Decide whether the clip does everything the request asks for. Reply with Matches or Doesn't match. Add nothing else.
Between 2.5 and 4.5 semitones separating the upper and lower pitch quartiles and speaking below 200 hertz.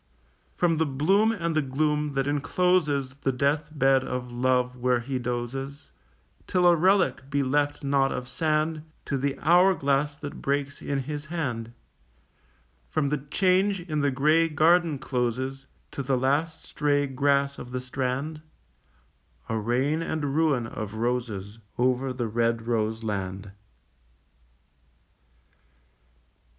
Matches